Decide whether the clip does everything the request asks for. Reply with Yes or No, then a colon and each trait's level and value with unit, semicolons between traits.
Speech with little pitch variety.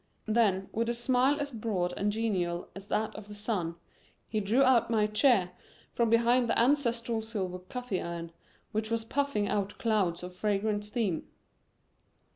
No: average, 3.2 semitones